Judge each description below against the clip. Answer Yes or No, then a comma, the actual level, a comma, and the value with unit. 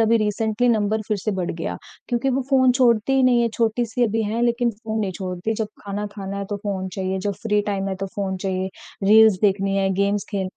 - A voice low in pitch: No, high, 210 Hz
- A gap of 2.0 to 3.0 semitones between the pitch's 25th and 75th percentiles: Yes, average, 2.7 semitones